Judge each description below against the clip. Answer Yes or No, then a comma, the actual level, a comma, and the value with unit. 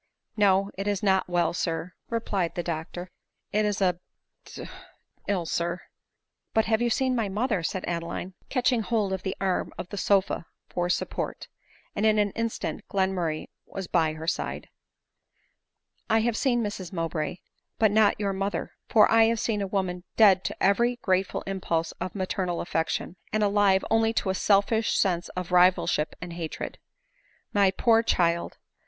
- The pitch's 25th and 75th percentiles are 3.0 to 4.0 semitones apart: Yes, average, 3.3 semitones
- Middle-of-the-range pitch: No, high, 195 Hz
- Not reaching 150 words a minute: No, average, 170 wpm